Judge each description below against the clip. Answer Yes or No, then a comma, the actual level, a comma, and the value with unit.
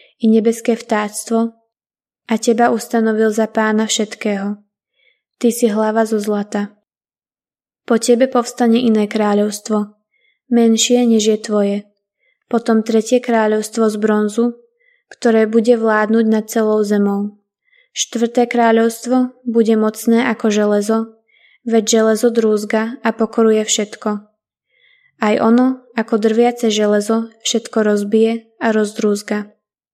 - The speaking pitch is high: Yes, high, 225 Hz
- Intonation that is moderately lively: No, narrow, 1.6 semitones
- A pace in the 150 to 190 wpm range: No, slow, 110 wpm